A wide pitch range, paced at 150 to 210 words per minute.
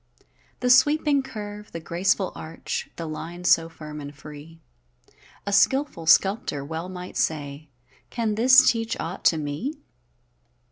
No: wide, 6.3 semitones; slow, 135 wpm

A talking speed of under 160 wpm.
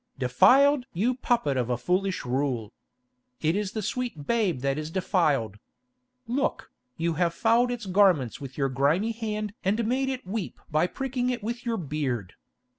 No: average, 165 wpm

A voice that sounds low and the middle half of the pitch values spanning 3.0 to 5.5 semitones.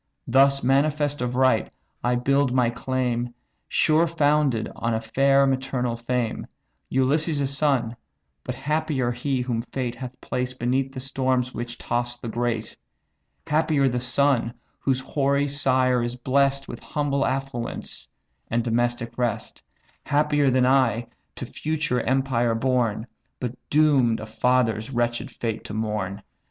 No: low, 130 Hz; narrow, 2.5 semitones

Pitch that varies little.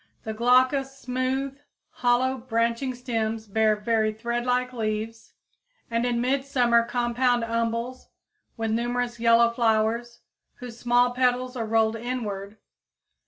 Yes: narrow, 1.8 semitones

